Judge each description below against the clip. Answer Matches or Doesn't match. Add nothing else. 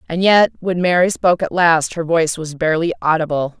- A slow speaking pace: Doesn't match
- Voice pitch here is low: Doesn't match